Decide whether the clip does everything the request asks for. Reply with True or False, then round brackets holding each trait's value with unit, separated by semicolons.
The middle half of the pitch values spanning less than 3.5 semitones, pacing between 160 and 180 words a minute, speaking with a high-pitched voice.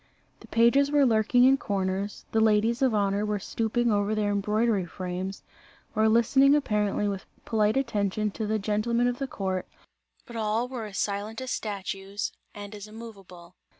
True (2.7 semitones; 165 wpm; 215 Hz)